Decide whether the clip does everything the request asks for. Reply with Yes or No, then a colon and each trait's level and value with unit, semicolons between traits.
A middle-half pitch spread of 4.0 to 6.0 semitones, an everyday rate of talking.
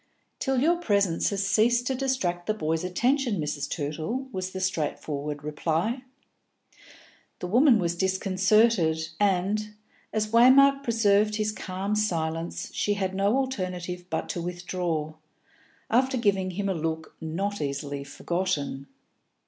No: average, 4.8 semitones; slow, 130 wpm